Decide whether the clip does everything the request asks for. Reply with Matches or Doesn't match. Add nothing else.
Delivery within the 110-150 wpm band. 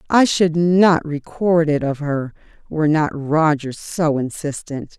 Matches